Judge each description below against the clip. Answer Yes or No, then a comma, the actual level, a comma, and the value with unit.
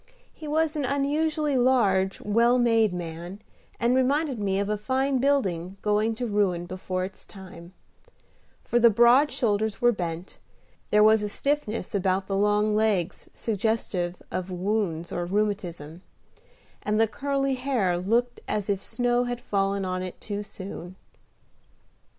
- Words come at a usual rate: Yes, average, 145 wpm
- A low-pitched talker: No, high, 210 Hz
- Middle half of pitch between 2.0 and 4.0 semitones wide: No, average, 4.5 semitones